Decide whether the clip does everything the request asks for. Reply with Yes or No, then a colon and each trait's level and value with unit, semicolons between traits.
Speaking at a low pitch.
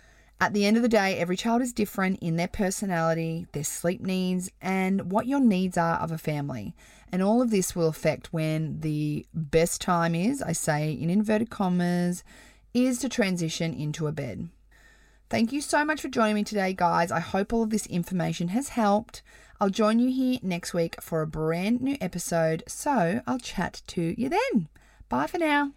No: medium, 185 Hz